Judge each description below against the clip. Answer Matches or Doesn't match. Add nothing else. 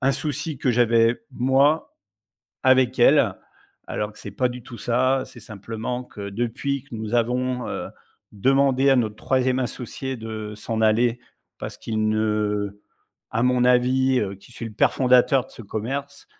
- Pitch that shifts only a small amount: Doesn't match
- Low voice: Matches